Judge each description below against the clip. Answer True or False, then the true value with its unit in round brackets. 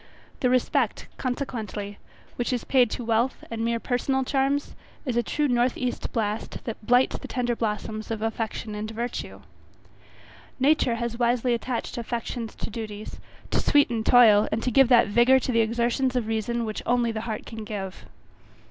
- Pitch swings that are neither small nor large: False (2.1 semitones)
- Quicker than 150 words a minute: True (170 wpm)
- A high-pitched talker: True (235 Hz)